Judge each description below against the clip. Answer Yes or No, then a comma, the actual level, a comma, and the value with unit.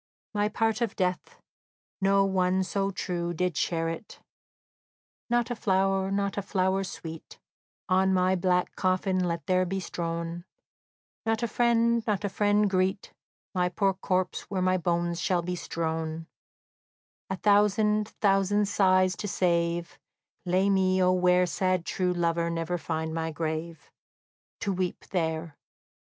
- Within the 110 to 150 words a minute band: Yes, average, 140 wpm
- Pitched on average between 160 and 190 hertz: Yes, medium, 185 Hz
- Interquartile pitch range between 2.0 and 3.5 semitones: Yes, narrow, 2.4 semitones